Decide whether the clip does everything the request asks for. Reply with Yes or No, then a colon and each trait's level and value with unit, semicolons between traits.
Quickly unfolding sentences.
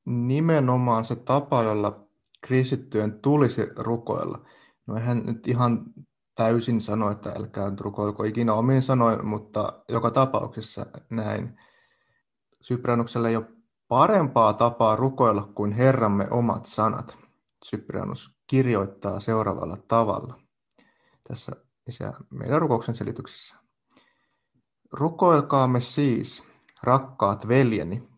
No: average, 100 wpm